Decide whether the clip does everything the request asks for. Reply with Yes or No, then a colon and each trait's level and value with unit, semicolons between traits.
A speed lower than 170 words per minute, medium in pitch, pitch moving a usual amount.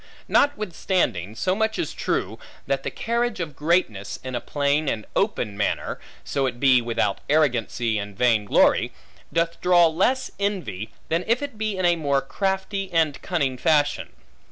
No: average, 160 wpm; medium, 155 Hz; wide, 7.7 semitones